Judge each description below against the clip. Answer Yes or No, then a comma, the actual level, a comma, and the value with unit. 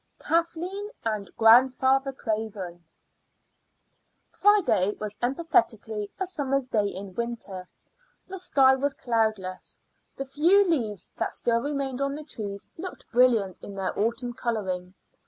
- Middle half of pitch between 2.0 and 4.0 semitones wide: No, average, 5.2 semitones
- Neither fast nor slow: No, slow, 120 wpm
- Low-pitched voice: No, high, 240 Hz